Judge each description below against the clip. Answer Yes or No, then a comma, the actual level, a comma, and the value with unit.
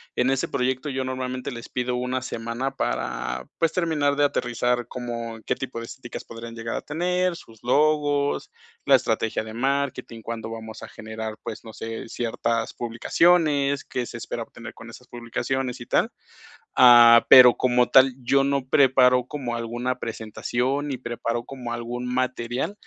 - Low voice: Yes, low, 125 Hz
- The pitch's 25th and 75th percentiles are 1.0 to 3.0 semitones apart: Yes, narrow, 2.6 semitones